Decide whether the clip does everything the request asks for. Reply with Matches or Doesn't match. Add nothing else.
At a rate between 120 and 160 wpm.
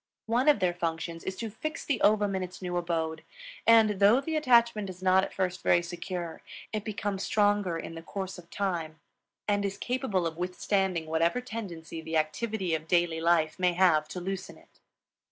Doesn't match